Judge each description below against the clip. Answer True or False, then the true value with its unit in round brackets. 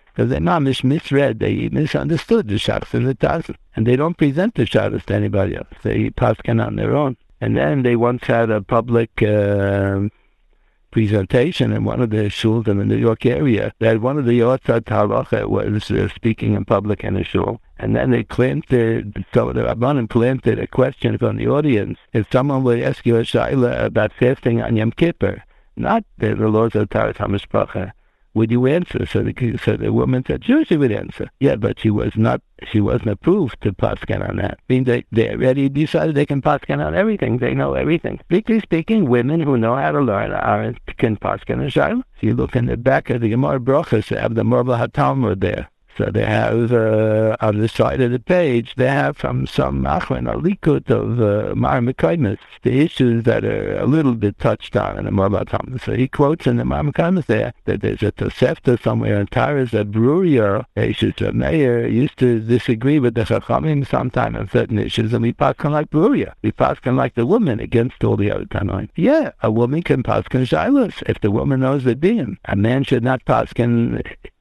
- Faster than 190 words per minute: True (205 wpm)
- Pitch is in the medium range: False (120 Hz)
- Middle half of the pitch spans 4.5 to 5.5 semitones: False (3.9 semitones)